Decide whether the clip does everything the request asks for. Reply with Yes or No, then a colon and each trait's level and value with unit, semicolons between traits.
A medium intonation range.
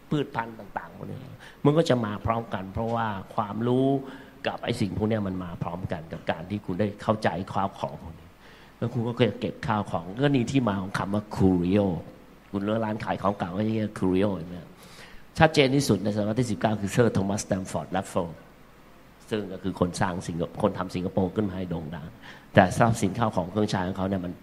Yes: average, 3.5 semitones